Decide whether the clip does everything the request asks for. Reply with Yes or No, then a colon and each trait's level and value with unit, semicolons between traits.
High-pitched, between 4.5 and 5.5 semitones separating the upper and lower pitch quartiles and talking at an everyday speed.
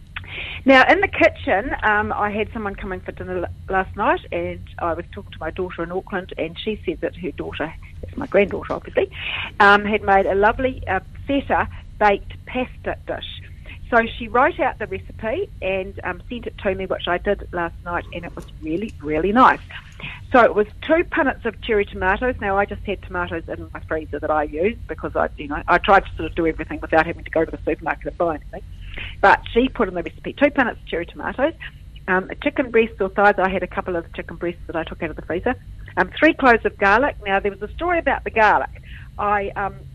No: high, 200 Hz; average, 4.8 semitones; fast, 225 wpm